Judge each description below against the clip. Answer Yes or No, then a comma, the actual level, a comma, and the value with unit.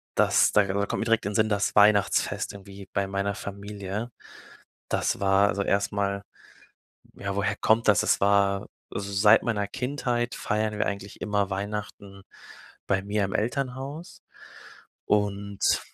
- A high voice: No, low, 100 Hz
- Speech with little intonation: Yes, narrow, 1.3 semitones